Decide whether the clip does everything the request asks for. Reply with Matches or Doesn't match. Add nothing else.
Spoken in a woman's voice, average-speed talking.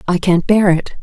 Doesn't match